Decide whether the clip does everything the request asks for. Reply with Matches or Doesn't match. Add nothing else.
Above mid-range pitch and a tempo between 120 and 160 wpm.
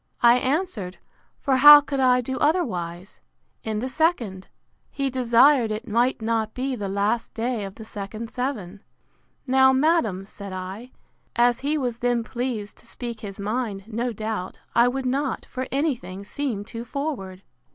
Matches